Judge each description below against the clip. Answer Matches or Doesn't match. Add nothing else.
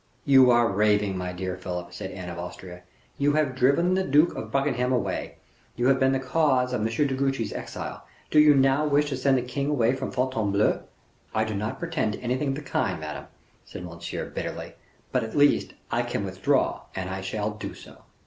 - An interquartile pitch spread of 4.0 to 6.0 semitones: Matches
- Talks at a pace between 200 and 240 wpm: Matches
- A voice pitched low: Matches